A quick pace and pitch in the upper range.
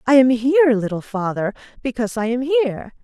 No: average, 180 wpm; high, 235 Hz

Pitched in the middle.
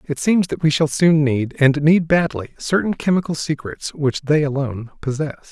Yes: medium, 150 Hz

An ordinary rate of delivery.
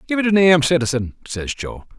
No: fast, 210 wpm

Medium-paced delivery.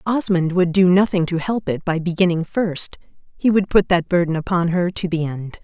No: fast, 215 wpm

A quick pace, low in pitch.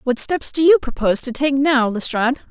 No: fast, 215 wpm; very high, 270 Hz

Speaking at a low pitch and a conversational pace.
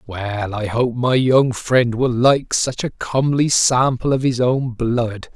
Yes: low, 125 Hz; average, 180 wpm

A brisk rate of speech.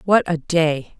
No: average, 180 wpm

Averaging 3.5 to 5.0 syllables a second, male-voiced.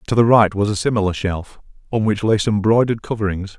No: 6.1 syllables/s; male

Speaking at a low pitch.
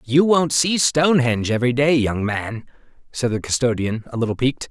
Yes: low, 130 Hz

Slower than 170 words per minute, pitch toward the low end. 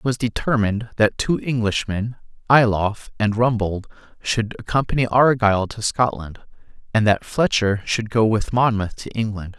Yes: average, 145 wpm; low, 110 Hz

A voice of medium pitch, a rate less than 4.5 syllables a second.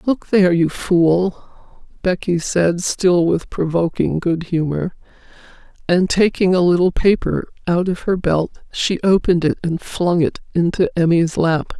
Yes: medium, 175 Hz; 4.1 syllables/s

